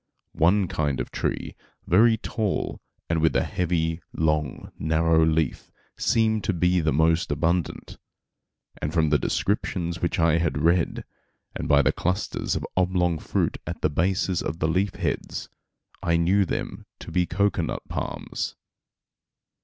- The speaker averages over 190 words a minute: No, average, 145 wpm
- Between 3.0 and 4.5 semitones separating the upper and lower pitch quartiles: No, narrow, 2.4 semitones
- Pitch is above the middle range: No, very low, 85 Hz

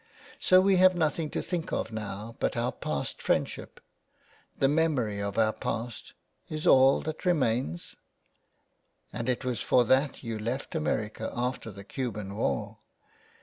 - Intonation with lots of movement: Yes, wide, 5.8 semitones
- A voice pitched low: Yes, low, 125 Hz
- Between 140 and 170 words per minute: Yes, average, 150 wpm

